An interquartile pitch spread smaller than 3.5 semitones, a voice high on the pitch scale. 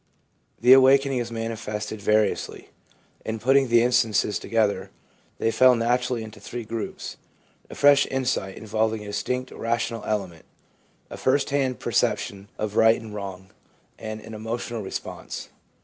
No: average, 2.8 semitones; low, 115 Hz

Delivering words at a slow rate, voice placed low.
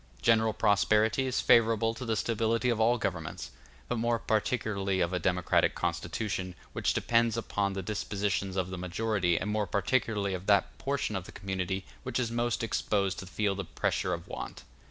No: average, 175 wpm; low, 105 Hz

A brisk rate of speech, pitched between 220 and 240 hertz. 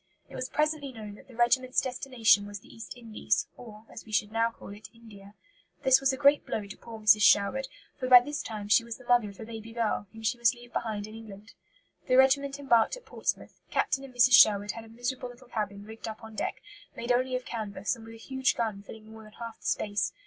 Yes: fast, 240 wpm; high, 230 Hz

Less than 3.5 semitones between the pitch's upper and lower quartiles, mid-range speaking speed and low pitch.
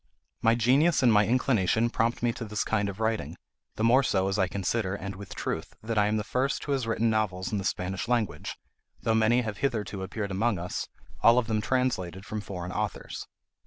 No: average, 3.1 semitones; fast, 210 wpm; low, 110 Hz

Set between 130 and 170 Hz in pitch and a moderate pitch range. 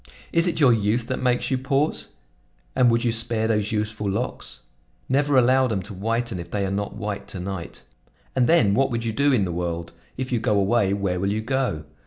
No: low, 115 Hz; average, 4.2 semitones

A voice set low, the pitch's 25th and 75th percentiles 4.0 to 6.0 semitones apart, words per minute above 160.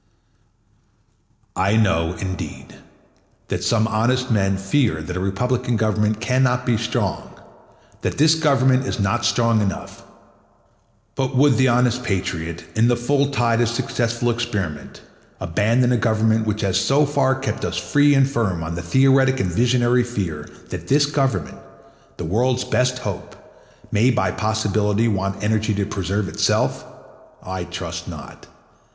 No: low, 115 Hz; average, 4.5 semitones; average, 145 wpm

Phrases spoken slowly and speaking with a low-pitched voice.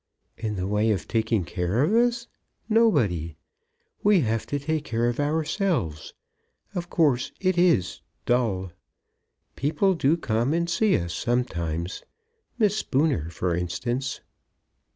Yes: slow, 130 wpm; low, 125 Hz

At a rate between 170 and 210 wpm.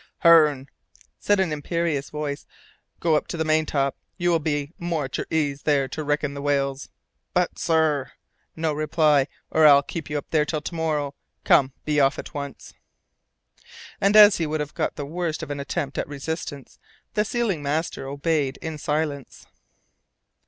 Yes: average, 175 wpm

